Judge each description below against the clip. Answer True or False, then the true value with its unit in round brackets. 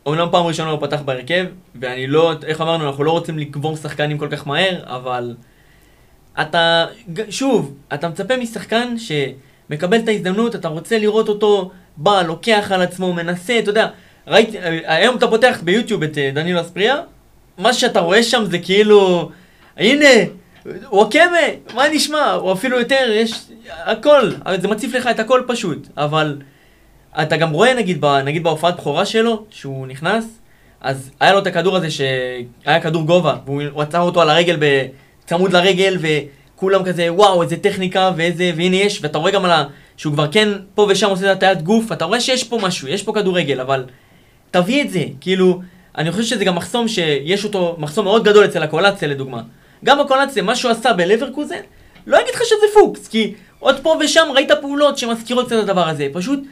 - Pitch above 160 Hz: True (185 Hz)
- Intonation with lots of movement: True (6.2 semitones)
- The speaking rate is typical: False (180 wpm)